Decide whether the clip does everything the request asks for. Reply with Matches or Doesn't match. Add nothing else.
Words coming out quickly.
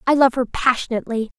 Doesn't match